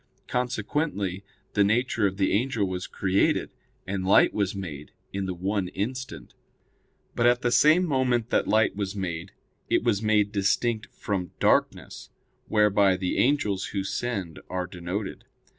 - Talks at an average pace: Yes, average, 145 wpm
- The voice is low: Yes, low, 100 Hz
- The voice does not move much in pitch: No, average, 3.9 semitones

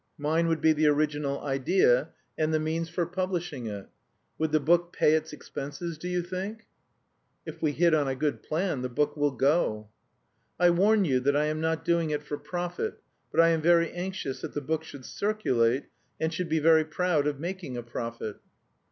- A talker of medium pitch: Yes, medium, 155 Hz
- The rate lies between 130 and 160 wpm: No, average, 195 wpm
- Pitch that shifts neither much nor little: Yes, average, 3.2 semitones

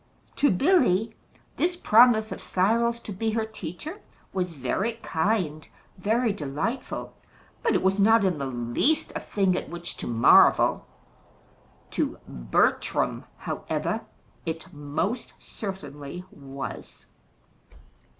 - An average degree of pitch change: No, wide, 6.5 semitones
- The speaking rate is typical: No, slow, 115 wpm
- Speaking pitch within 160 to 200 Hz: Yes, high, 190 Hz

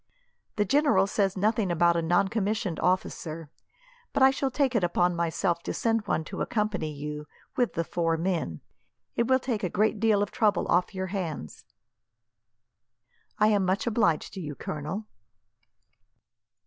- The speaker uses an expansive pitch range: No, average, 4.3 semitones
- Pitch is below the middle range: No, high, 190 Hz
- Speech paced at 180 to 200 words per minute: No, average, 155 wpm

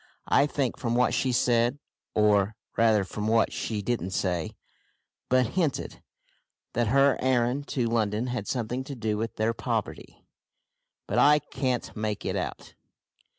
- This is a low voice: Yes, low, 120 Hz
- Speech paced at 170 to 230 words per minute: No, average, 150 wpm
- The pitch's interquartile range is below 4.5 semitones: Yes, average, 3.1 semitones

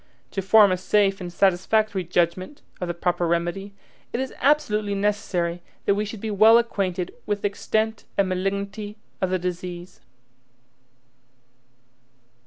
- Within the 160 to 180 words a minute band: No, average, 140 wpm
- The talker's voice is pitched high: Yes, high, 195 Hz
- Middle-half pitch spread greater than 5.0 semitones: No, average, 2.7 semitones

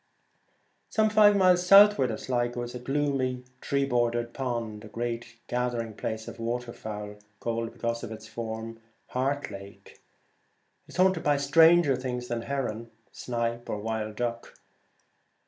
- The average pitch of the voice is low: Yes, low, 120 Hz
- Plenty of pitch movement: No, average, 3.3 semitones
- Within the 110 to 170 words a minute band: Yes, average, 160 wpm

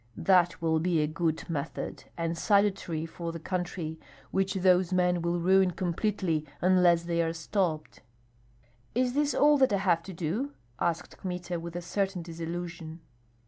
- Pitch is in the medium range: Yes, medium, 175 Hz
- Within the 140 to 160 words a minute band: Yes, average, 155 wpm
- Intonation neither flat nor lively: No, narrow, 2.3 semitones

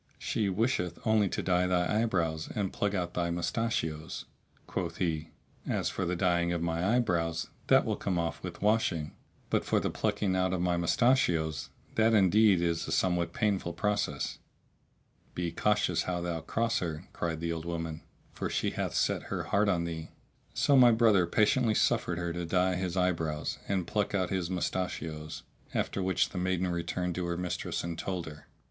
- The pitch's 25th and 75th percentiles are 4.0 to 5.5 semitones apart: No, average, 2.9 semitones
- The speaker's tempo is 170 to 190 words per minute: Yes, average, 180 wpm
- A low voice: Yes, very low, 90 Hz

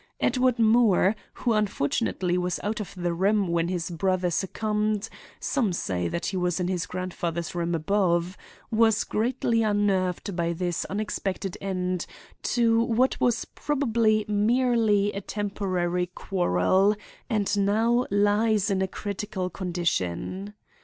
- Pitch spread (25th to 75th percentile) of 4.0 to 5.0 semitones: No, average, 3.3 semitones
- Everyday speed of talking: No, slow, 125 wpm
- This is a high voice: Yes, high, 200 Hz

